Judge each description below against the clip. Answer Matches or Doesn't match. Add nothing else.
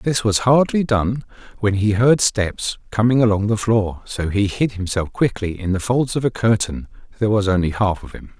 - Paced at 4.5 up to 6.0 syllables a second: Matches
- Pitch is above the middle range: Doesn't match